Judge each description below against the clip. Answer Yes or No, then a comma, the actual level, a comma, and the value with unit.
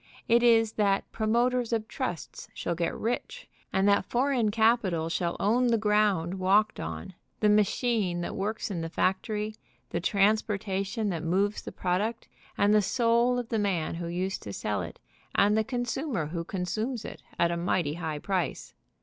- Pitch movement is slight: No, average, 4.2 semitones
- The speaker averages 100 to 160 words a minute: No, average, 170 wpm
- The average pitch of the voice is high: Yes, high, 205 Hz